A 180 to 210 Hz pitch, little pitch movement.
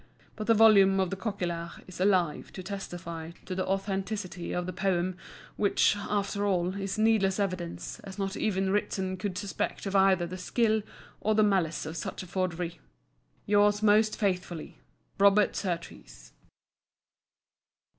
Yes: high, 190 Hz; narrow, 2.2 semitones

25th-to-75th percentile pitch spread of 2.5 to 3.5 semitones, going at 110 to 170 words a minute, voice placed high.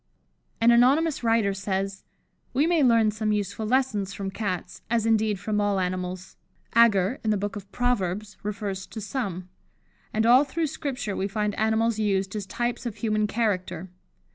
Yes: average, 3.1 semitones; average, 165 wpm; high, 215 Hz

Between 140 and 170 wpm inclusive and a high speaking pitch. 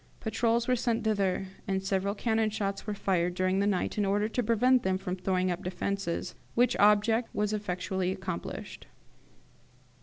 Yes: average, 160 wpm; high, 200 Hz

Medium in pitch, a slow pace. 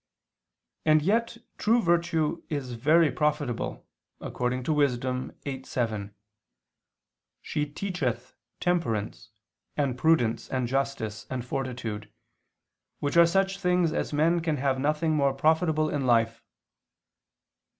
Yes: medium, 145 Hz; slow, 110 wpm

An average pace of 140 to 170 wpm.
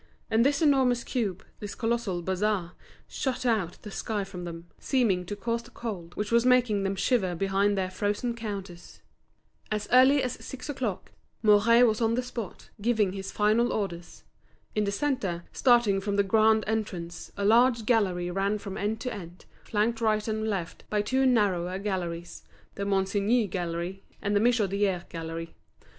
Yes: average, 165 wpm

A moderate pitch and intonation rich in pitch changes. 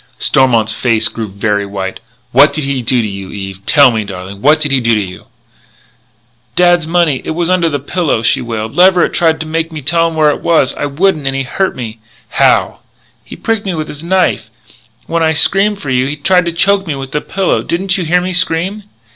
Yes: medium, 150 Hz; wide, 7.0 semitones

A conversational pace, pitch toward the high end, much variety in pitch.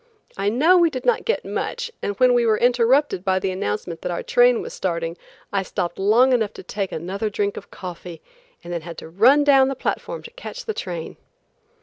No: fast, 215 wpm; high, 210 Hz; wide, 6.6 semitones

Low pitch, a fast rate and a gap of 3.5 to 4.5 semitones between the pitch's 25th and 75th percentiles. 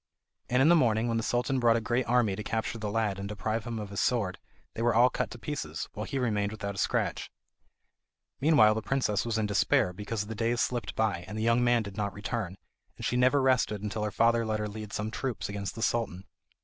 No: low, 110 Hz; fast, 240 wpm; narrow, 2.5 semitones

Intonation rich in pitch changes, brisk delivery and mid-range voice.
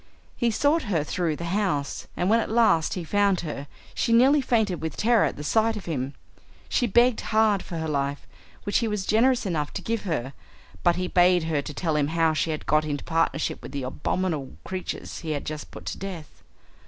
Yes: wide, 6.0 semitones; fast, 210 wpm; medium, 175 Hz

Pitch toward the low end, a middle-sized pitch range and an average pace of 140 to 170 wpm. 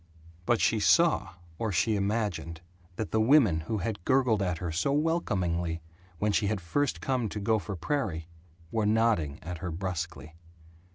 Yes: low, 100 Hz; average, 4.8 semitones; average, 160 wpm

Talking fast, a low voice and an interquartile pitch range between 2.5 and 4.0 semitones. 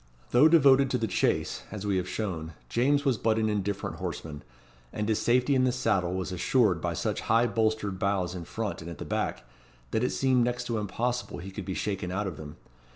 No: fast, 220 wpm; low, 105 Hz; average, 4.9 semitones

